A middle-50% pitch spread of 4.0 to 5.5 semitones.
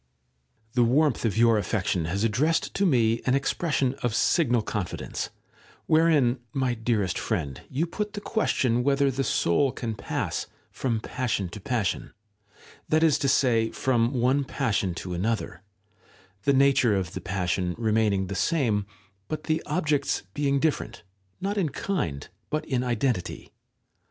Yes: average, 5.1 semitones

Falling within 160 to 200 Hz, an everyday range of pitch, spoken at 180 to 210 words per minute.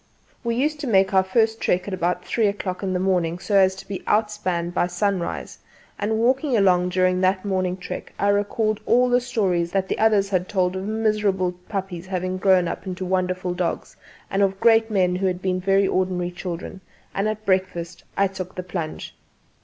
No: high, 190 Hz; narrow, 2.2 semitones; average, 195 wpm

